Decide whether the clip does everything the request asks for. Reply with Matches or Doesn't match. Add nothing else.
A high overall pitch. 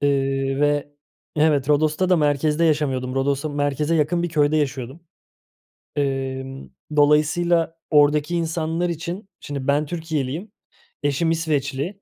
Doesn't match